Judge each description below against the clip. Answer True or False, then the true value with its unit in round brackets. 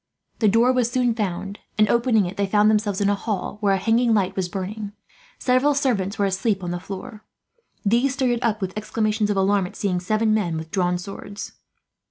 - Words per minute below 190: False (205 wpm)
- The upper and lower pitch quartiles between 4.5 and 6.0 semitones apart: False (2.8 semitones)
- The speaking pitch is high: True (205 Hz)